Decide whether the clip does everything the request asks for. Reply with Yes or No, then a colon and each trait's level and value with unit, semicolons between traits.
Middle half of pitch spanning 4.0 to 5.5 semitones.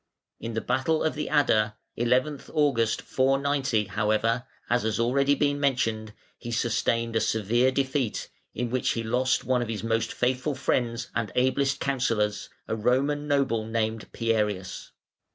No: average, 3.4 semitones